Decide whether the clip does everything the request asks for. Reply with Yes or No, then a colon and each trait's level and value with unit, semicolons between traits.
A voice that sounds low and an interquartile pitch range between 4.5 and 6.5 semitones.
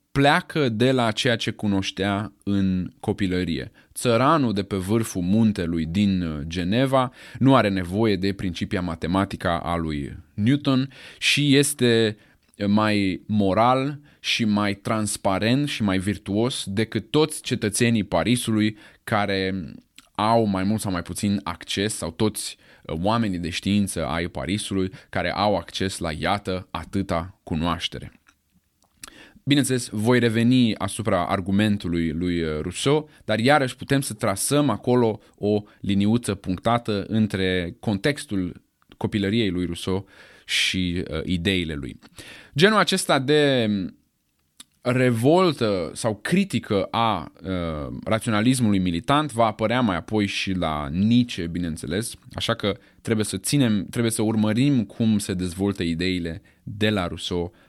No: low, 105 Hz; average, 4.0 semitones